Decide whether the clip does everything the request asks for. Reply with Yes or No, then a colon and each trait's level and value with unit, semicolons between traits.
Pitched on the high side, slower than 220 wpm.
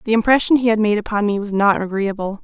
No: high, 210 Hz; fast, 245 wpm